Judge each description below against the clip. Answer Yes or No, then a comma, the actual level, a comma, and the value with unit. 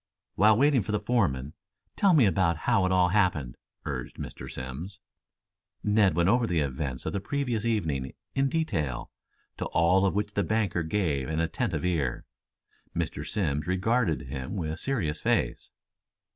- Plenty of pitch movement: Yes, wide, 5.7 semitones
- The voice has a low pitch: Yes, very low, 90 Hz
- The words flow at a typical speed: Yes, average, 160 wpm